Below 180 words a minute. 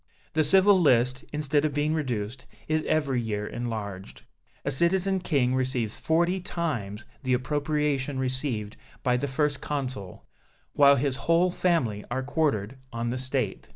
Yes: average, 145 wpm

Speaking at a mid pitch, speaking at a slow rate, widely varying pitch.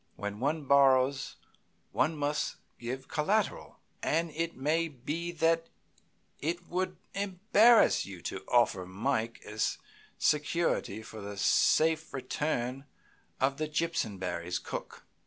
Yes: medium, 145 Hz; slow, 115 wpm; wide, 5.7 semitones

